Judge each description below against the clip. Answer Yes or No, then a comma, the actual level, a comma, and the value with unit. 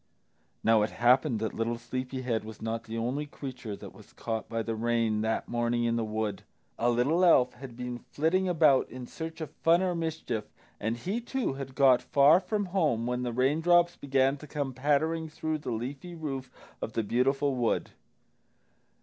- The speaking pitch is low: Yes, low, 130 Hz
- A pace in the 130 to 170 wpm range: No, average, 185 wpm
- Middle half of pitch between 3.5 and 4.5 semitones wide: No, average, 5.0 semitones